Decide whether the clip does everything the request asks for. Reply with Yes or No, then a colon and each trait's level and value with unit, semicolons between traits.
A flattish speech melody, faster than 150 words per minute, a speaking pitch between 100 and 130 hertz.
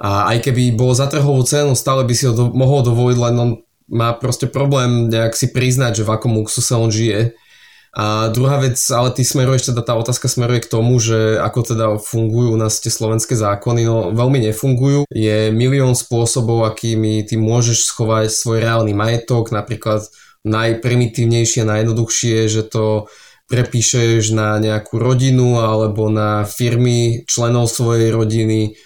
Yes: narrow, 2.0 semitones; average, 160 wpm; low, 115 Hz